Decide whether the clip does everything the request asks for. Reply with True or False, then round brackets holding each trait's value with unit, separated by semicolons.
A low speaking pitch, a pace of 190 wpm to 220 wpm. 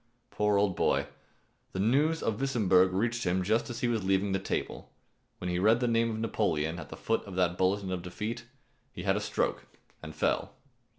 True (100 Hz; 200 wpm)